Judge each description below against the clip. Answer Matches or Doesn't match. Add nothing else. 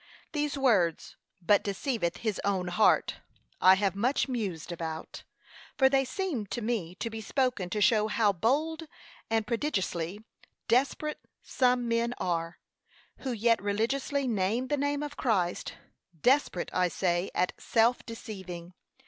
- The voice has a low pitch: Doesn't match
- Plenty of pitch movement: Matches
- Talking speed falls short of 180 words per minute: Matches